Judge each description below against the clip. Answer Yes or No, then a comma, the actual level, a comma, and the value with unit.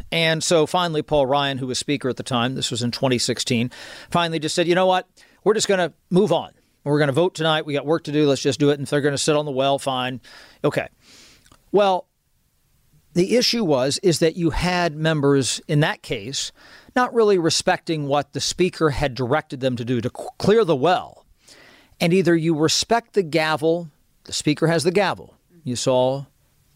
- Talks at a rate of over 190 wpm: Yes, fast, 205 wpm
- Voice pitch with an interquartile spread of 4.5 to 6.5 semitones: No, average, 4.0 semitones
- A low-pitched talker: No, medium, 155 Hz